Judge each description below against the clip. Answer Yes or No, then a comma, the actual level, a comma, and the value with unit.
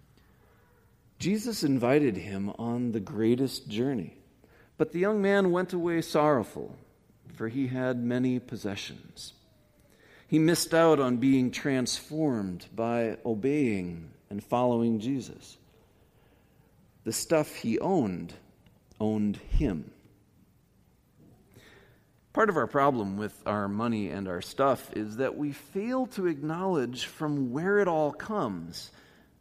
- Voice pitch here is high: No, low, 125 Hz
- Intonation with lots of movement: Yes, wide, 6.3 semitones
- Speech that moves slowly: Yes, slow, 115 wpm